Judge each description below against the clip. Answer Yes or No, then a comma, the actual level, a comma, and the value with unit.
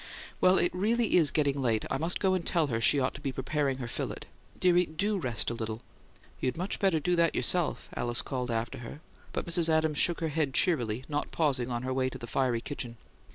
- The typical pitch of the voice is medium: Yes, medium, 145 Hz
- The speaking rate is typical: No, fast, 225 wpm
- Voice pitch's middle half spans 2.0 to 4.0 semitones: No, wide, 5.5 semitones